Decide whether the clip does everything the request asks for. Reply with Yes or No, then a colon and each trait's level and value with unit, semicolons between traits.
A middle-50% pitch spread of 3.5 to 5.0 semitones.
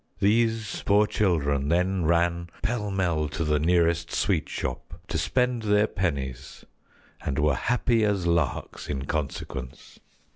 No: wide, 5.4 semitones